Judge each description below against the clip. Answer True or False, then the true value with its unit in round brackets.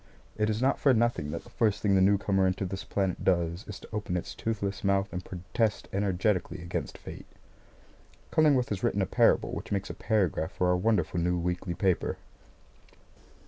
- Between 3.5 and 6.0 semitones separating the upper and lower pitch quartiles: False (3.0 semitones)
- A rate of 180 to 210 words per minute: True (185 wpm)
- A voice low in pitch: True (95 Hz)